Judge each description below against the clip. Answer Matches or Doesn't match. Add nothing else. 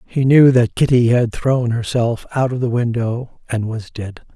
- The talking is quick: Doesn't match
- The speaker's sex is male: Matches